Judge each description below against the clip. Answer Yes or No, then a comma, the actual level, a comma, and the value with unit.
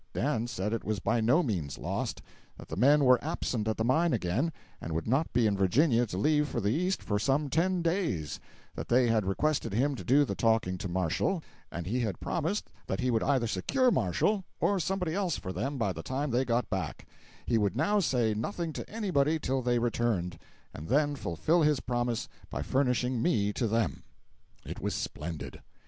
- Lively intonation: Yes, wide, 6.2 semitones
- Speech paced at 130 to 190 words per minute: No, average, 200 wpm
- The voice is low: Yes, low, 120 Hz